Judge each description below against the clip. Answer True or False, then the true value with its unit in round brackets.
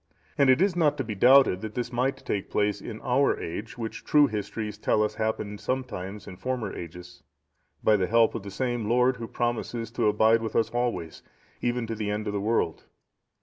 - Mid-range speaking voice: False (115 Hz)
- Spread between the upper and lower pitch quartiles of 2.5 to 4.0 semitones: True (3.0 semitones)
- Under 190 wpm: False (205 wpm)